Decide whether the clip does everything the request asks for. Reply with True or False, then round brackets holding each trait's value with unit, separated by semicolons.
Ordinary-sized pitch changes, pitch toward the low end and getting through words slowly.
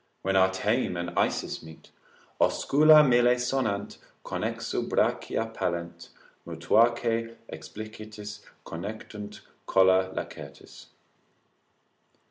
True (3.8 semitones; 105 Hz; 85 wpm)